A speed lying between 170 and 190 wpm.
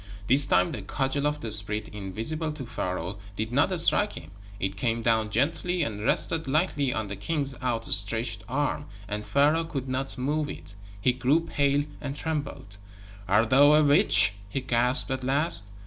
Yes: average, 175 wpm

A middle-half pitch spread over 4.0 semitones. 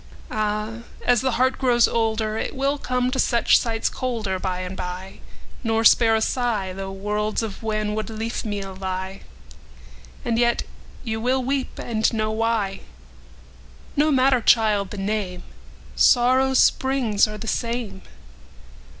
No: average, 2.9 semitones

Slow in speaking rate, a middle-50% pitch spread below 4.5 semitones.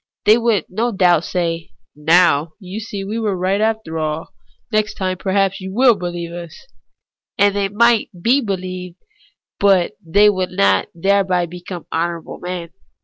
No: average, 160 wpm; average, 3.0 semitones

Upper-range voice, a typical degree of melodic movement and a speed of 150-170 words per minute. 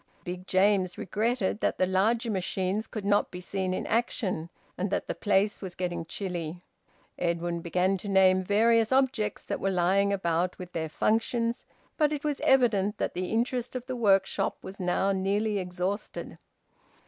Yes: high, 195 Hz; average, 3.4 semitones; average, 165 wpm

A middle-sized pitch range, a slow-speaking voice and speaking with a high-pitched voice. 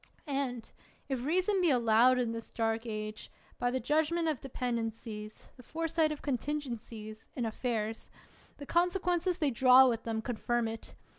No: average, 5.0 semitones; average, 160 wpm; very high, 250 Hz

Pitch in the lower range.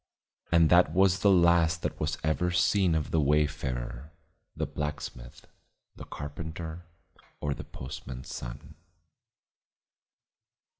Yes: very low, 80 Hz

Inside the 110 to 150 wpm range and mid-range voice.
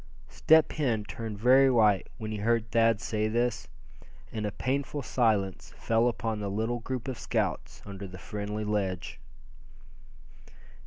No: average, 145 wpm; low, 110 Hz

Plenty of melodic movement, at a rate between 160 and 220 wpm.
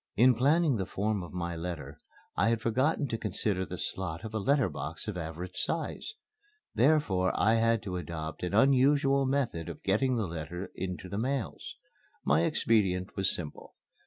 Yes: wide, 6.3 semitones; average, 170 wpm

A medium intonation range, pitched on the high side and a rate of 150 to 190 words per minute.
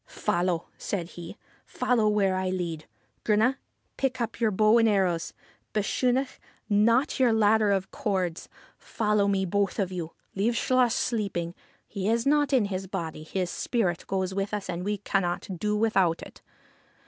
Yes: average, 3.5 semitones; high, 200 Hz; average, 170 wpm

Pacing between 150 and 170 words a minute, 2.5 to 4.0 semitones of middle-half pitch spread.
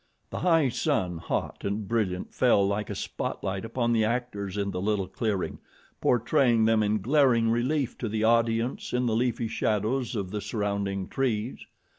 Yes: average, 165 wpm; average, 3.1 semitones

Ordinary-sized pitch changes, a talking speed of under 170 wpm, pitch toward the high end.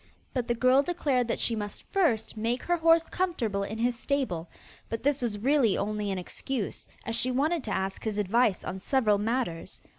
No: average, 4.6 semitones; average, 190 wpm; high, 235 Hz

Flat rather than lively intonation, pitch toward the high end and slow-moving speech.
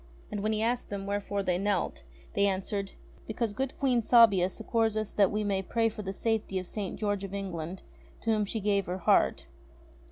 No: narrow, 2.3 semitones; high, 205 Hz; average, 200 wpm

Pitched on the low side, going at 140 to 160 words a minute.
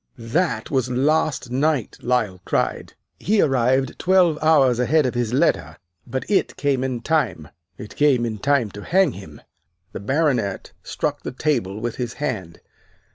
Yes: low, 130 Hz; average, 155 wpm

